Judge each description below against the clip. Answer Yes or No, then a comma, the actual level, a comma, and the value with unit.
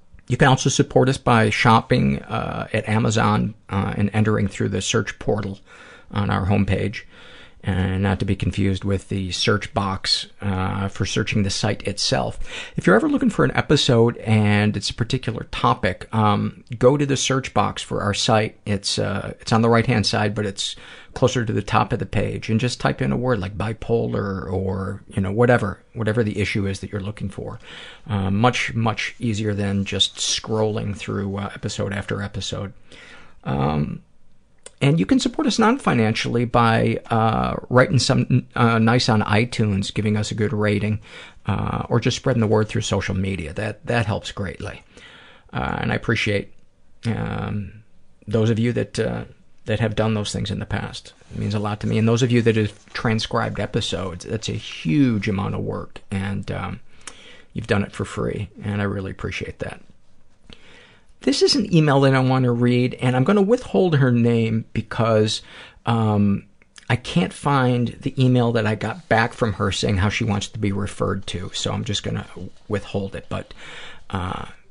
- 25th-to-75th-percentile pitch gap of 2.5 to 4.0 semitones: Yes, average, 3.1 semitones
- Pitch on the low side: Yes, low, 110 Hz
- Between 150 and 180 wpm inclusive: No, average, 190 wpm